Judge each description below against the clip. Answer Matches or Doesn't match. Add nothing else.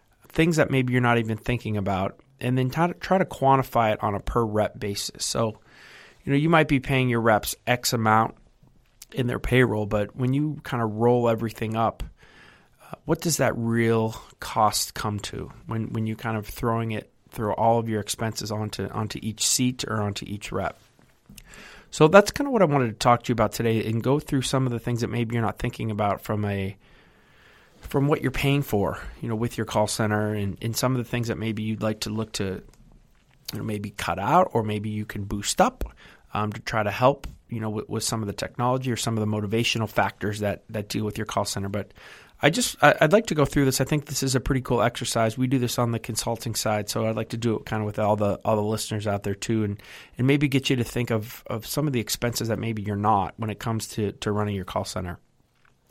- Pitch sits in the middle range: Doesn't match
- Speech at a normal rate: Doesn't match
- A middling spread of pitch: Matches